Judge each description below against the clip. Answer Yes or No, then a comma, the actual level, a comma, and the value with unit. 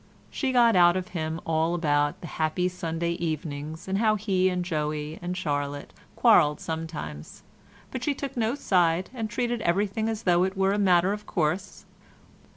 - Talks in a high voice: No, medium, 175 Hz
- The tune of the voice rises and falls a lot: No, average, 4.3 semitones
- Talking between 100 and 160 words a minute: No, average, 170 wpm